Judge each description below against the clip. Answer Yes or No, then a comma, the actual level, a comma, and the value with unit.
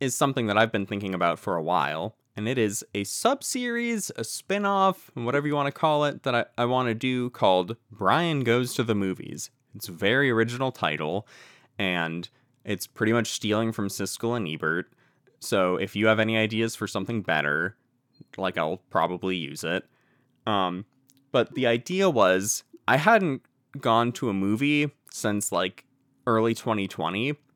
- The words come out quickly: No, average, 170 wpm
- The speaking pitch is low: Yes, low, 115 Hz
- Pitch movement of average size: Yes, average, 4.8 semitones